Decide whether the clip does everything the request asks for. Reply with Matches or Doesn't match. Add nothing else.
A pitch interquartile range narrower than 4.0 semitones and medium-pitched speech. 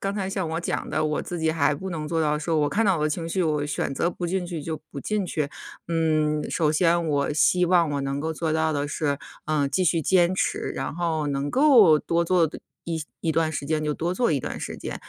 Matches